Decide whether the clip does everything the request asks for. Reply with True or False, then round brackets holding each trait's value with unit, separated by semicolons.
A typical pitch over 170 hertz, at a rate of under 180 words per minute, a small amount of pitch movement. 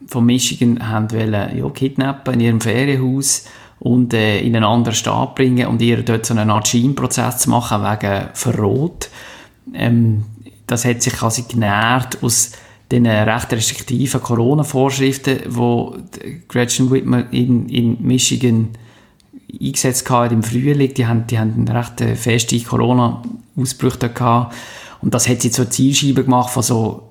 False (120 Hz; 140 wpm; 1.9 semitones)